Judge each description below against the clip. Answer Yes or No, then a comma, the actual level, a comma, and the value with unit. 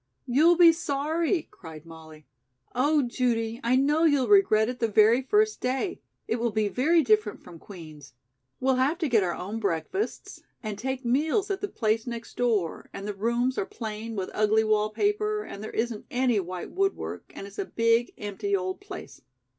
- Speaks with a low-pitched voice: No, high, 235 Hz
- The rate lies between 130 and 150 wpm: No, average, 185 wpm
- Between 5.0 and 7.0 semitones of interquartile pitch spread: Yes, wide, 5.6 semitones